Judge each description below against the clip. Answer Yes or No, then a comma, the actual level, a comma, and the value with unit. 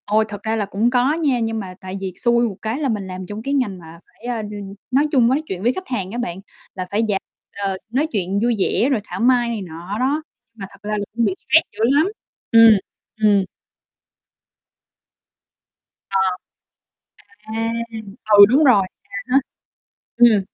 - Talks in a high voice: Yes, high, 220 Hz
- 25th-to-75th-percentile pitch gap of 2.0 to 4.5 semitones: Yes, average, 3.8 semitones